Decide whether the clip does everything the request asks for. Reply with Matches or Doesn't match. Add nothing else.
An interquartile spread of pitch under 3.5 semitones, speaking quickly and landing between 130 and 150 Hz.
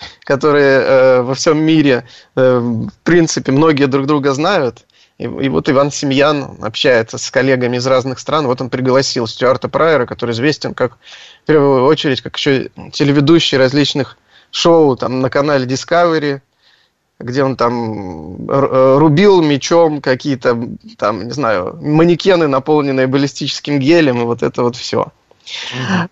Doesn't match